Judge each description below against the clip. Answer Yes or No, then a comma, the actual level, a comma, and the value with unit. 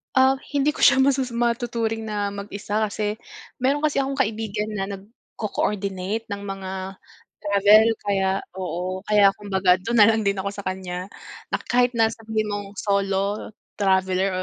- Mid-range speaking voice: No, high, 205 Hz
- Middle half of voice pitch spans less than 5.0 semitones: Yes, narrow, 2.5 semitones